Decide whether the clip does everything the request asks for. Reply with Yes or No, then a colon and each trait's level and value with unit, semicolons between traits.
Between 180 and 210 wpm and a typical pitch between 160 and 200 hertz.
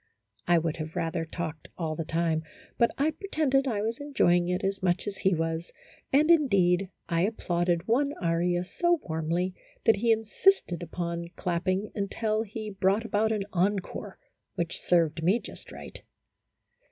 No: average, 155 wpm; medium, 185 Hz